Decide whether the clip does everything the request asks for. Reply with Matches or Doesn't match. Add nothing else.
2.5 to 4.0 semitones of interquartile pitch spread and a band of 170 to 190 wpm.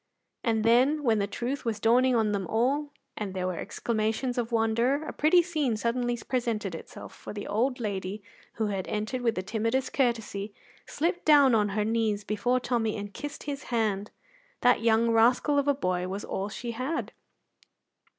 Matches